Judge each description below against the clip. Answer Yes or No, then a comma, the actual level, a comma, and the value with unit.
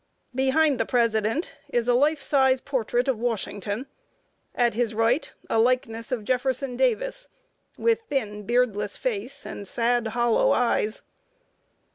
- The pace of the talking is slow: Yes, slow, 130 wpm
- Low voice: No, high, 245 Hz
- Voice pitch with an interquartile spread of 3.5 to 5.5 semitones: No, average, 2.9 semitones